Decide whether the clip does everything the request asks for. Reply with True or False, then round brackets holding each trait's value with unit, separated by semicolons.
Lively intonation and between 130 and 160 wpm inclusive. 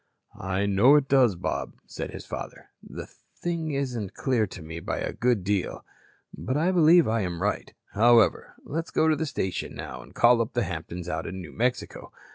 False (6.8 semitones; 195 wpm)